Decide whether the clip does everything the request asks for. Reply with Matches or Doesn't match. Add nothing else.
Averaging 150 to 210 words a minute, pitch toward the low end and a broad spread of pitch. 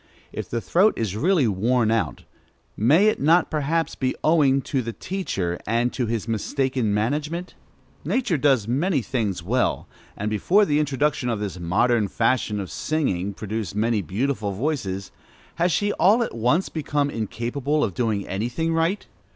Matches